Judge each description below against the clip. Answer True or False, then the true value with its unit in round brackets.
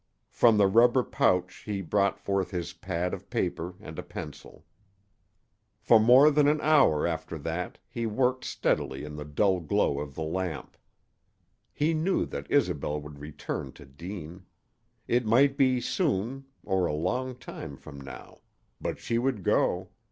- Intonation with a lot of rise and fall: True (7.9 semitones)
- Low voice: True (95 Hz)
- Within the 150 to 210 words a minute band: True (160 wpm)